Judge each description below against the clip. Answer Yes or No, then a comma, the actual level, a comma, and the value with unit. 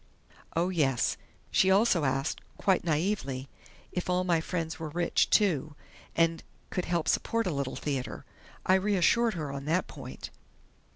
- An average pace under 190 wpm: Yes, average, 150 wpm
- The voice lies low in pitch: No, medium, 165 Hz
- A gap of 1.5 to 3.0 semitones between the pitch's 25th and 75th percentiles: No, average, 4.1 semitones